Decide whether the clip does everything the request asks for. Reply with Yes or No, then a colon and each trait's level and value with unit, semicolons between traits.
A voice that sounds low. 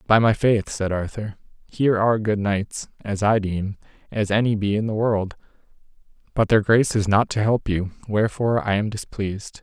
Yes: low, 105 Hz